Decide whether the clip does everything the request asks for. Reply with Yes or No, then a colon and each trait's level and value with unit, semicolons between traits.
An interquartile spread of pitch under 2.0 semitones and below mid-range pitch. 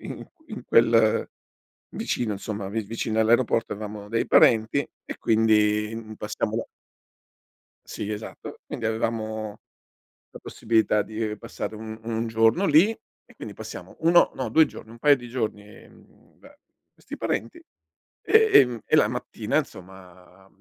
Yes: narrow, 1.6 semitones; low, 110 Hz